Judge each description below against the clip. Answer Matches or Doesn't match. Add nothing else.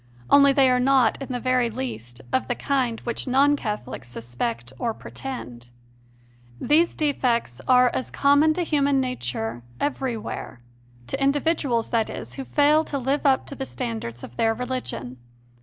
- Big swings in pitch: Doesn't match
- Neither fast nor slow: Matches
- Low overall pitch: Doesn't match